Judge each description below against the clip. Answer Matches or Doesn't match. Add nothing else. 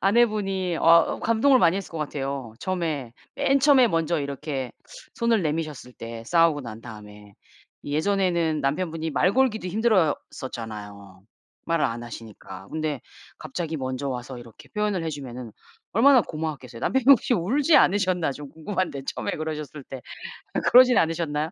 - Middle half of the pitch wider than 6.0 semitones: Matches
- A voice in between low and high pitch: Matches